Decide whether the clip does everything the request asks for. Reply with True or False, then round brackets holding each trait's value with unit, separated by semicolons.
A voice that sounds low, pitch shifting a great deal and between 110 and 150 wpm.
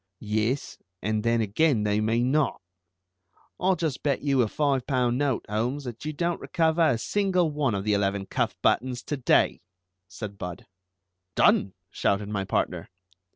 False (120 Hz; 5.7 semitones; 160 wpm)